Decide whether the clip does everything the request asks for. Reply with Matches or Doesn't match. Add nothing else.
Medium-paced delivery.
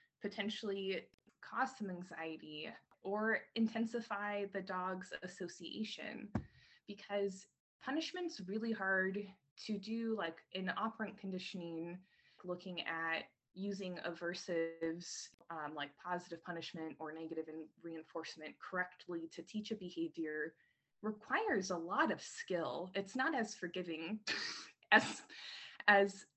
Doesn't match